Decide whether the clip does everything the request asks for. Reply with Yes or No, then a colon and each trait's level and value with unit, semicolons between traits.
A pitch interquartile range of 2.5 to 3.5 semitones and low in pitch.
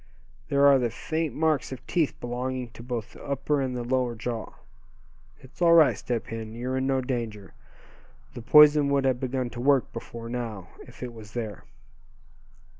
Yes: average, 2.9 semitones; low, 125 Hz